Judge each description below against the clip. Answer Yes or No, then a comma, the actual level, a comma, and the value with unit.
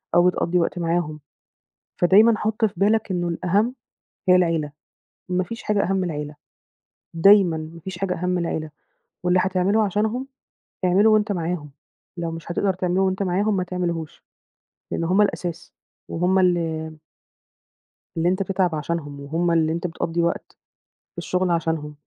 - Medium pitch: Yes, medium, 180 Hz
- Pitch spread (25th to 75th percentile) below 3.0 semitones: Yes, narrow, 2.6 semitones